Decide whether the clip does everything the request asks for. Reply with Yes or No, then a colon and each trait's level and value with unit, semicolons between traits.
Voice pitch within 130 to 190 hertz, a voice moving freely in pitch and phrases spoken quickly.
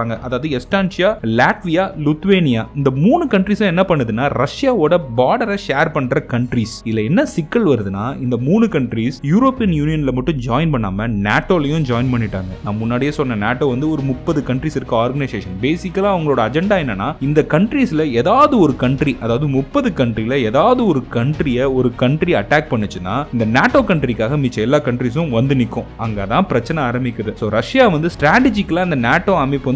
Yes: medium, 140 Hz; wide, 6.0 semitones; fast, 155 wpm